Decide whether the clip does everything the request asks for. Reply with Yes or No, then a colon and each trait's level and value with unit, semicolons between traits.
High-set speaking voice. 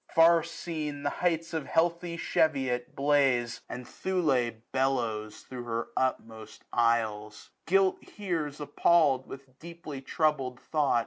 No: medium, 140 Hz